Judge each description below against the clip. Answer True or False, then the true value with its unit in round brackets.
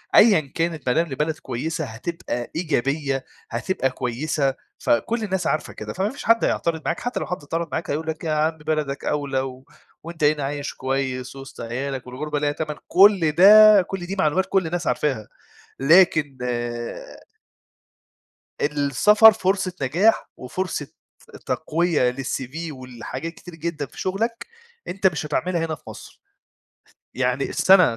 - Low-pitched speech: False (155 Hz)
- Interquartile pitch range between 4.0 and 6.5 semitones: True (4.7 semitones)